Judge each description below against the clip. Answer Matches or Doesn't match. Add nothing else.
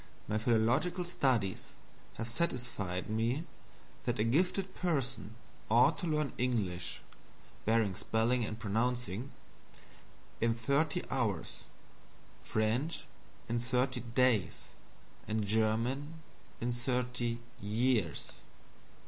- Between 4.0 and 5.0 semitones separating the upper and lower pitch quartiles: Doesn't match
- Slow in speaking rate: Matches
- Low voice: Matches